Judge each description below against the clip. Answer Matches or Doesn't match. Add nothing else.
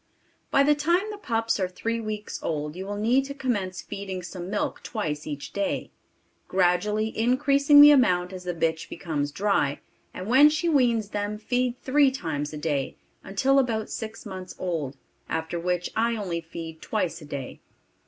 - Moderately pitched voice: Doesn't match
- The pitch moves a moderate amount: Doesn't match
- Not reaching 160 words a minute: Doesn't match